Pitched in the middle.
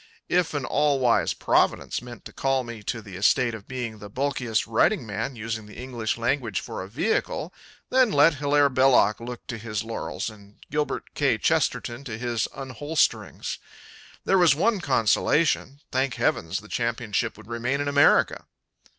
No: low, 125 Hz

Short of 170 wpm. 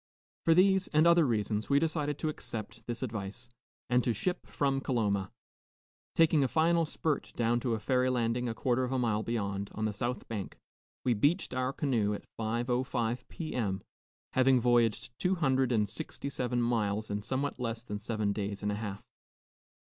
No: average, 180 wpm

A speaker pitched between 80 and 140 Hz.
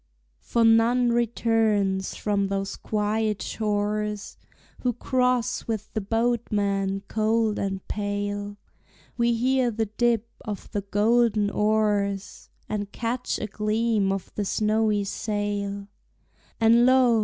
No: high, 215 Hz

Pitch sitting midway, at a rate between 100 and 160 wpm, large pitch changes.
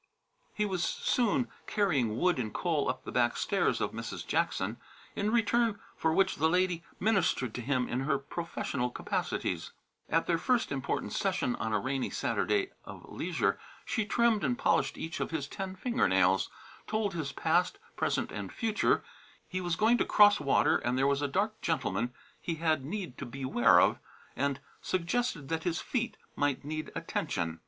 No: medium, 160 Hz; average, 175 wpm; wide, 7.2 semitones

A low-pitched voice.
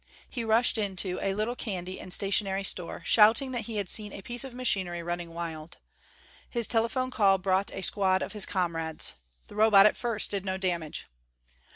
No: high, 195 Hz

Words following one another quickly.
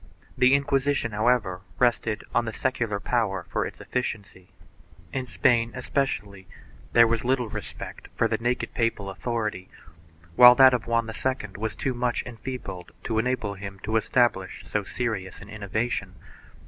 No: average, 150 wpm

